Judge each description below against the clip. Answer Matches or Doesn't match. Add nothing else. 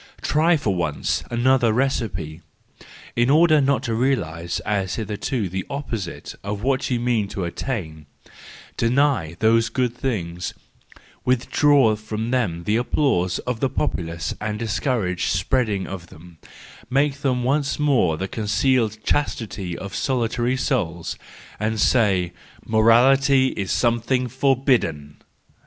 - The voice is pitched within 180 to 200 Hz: Doesn't match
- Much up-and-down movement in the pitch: Matches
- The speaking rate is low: Matches